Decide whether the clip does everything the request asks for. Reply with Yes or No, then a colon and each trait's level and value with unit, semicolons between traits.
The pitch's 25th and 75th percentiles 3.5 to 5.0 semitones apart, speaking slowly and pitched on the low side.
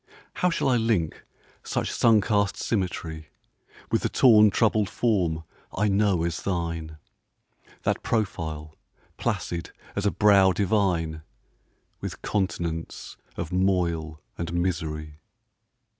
Yes: average, 4.2 semitones; slow, 115 wpm; very low, 90 Hz